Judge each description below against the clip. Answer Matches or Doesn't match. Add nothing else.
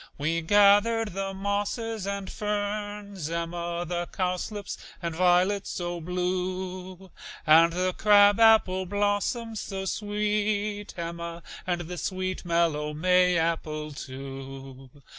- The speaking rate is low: Matches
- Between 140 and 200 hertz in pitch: Matches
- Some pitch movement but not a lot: Matches